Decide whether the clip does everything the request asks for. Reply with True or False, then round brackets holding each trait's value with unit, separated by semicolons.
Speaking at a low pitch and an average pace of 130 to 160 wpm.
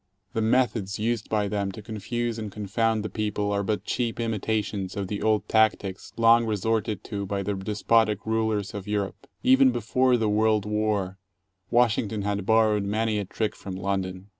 False (105 Hz; 170 wpm)